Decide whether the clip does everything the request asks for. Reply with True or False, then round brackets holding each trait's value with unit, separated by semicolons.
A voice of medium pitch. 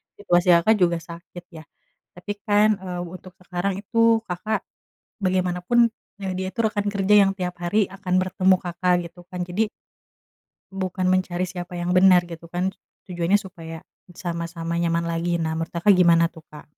True (180 Hz)